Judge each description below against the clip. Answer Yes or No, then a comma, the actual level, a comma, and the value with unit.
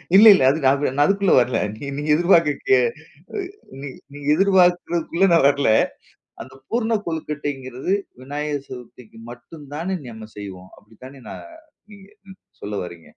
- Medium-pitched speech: Yes, medium, 145 Hz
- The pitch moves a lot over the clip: Yes, wide, 6.2 semitones